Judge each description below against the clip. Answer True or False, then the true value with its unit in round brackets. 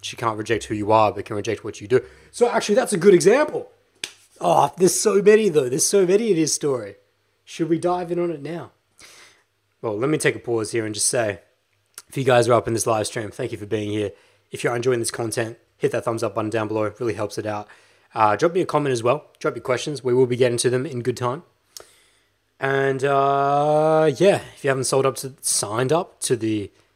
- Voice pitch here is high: False (125 Hz)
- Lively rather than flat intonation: True (6.9 semitones)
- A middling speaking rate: False (245 wpm)